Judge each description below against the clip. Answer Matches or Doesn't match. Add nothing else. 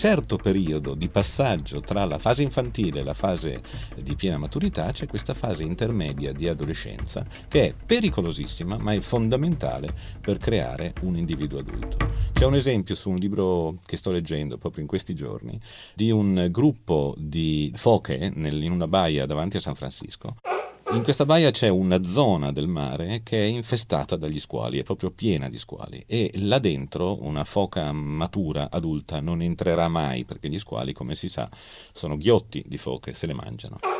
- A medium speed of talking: Doesn't match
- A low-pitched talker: Matches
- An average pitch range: Doesn't match